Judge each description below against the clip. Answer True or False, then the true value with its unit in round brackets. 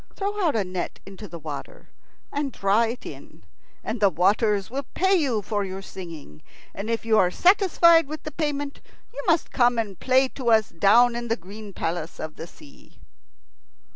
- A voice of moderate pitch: False (225 Hz)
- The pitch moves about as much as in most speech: False (6.5 semitones)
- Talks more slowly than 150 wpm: False (185 wpm)